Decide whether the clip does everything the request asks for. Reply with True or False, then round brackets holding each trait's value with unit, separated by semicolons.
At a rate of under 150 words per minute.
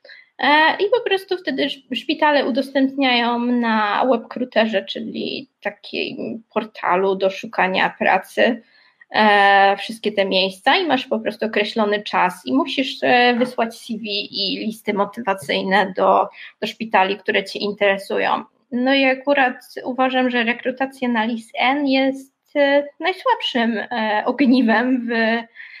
True (110 wpm)